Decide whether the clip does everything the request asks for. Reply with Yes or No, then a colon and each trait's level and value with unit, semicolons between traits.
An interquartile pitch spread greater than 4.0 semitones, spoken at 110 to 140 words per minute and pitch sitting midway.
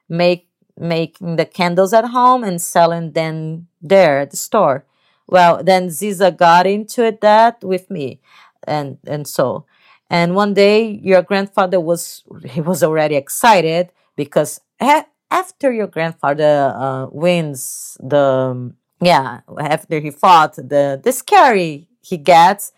Yes: average, 4.6 semitones; slow, 135 wpm; medium, 175 Hz